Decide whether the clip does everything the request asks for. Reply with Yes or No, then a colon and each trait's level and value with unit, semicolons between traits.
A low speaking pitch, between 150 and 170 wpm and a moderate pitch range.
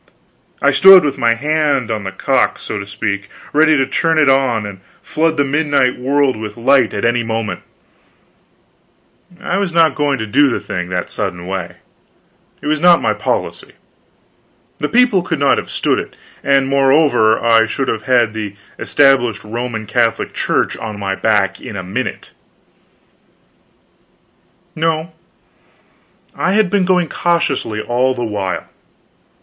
No: low, 130 Hz; average, 155 wpm; wide, 5.9 semitones